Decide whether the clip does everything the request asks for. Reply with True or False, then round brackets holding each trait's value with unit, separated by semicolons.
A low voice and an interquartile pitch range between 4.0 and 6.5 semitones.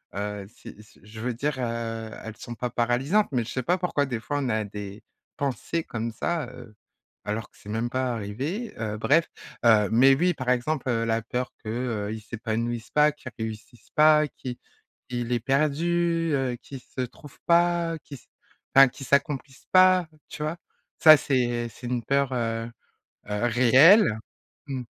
True (125 Hz; 4.7 semitones)